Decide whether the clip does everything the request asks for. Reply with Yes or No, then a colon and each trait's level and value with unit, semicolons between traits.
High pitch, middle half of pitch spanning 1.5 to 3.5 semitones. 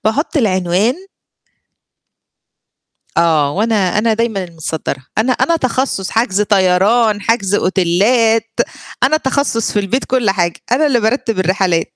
No: high, 215 Hz; average, 4.3 semitones